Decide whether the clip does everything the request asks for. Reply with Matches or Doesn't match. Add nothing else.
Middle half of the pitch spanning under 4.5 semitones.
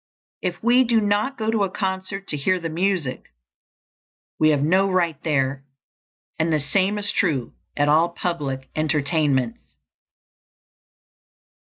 Doesn't match